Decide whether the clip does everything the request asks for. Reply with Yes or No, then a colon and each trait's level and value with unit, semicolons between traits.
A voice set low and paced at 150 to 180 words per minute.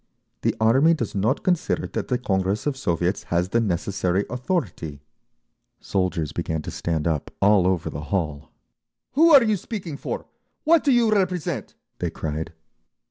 Yes: low, 100 Hz; average, 155 wpm